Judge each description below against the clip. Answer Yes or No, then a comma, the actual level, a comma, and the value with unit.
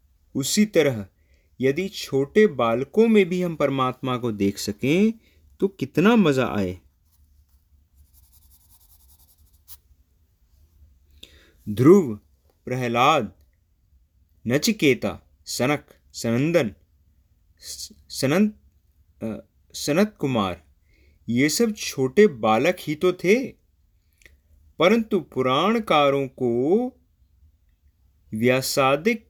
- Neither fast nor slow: No, slow, 70 wpm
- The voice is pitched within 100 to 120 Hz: Yes, low, 105 Hz